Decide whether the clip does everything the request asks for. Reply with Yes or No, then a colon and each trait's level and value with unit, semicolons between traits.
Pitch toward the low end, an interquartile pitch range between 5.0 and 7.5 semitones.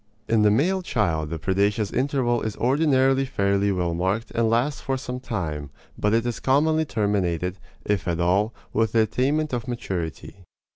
Yes: low, 110 Hz; wide, 5.5 semitones